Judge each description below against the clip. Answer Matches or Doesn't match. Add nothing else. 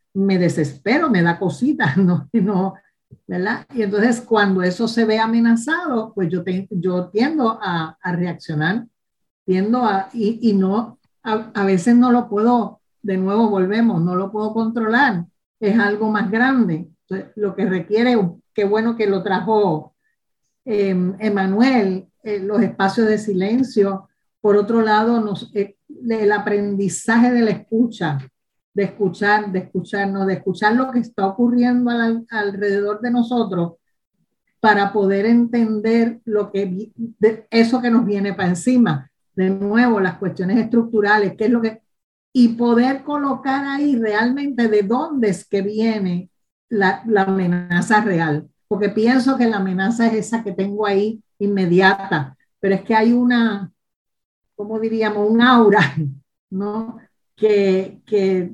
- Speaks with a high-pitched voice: Matches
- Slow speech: Doesn't match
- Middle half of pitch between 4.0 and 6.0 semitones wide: Doesn't match